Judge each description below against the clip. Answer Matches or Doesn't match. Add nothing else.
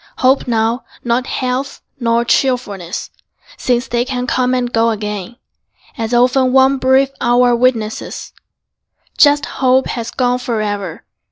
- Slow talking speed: Matches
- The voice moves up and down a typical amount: Doesn't match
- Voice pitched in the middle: Doesn't match